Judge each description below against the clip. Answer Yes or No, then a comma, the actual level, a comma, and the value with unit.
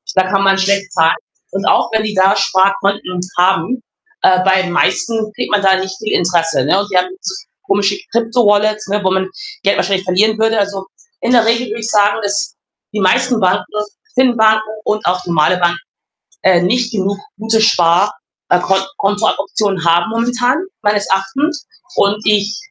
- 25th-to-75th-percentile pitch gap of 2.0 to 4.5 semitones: Yes, narrow, 2.6 semitones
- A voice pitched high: Yes, high, 200 Hz